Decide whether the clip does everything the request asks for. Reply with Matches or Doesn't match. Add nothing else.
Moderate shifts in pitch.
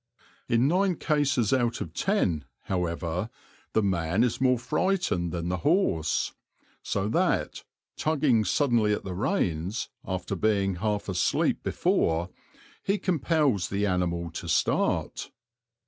Doesn't match